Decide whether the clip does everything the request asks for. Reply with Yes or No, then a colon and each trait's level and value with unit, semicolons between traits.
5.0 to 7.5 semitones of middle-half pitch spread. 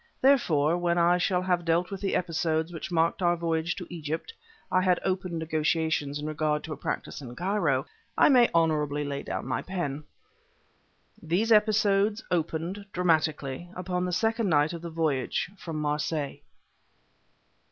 No: average, 2.9 semitones